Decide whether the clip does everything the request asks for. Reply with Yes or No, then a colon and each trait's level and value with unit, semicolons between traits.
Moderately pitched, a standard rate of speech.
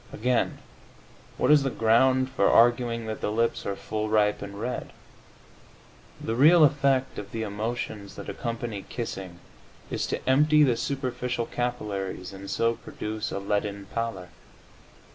No: low, 115 Hz; average, 145 wpm